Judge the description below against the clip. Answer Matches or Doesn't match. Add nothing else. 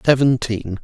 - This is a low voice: Matches